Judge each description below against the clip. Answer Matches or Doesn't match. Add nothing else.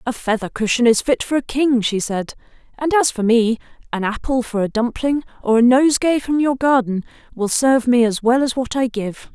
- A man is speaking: Doesn't match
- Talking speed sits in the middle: Doesn't match